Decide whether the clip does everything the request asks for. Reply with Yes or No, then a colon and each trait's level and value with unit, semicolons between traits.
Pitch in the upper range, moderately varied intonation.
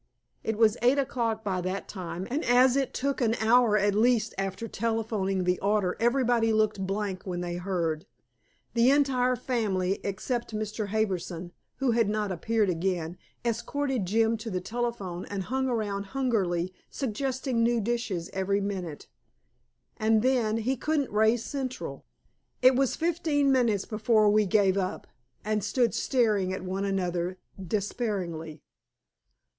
Yes: high, 215 Hz; average, 4.1 semitones